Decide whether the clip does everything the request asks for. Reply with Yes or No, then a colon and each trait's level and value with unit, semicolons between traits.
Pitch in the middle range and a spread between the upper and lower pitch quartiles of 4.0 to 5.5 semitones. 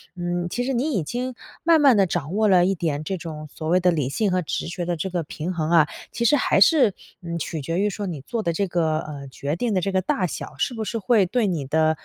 Yes: medium, 175 Hz; average, 4.8 semitones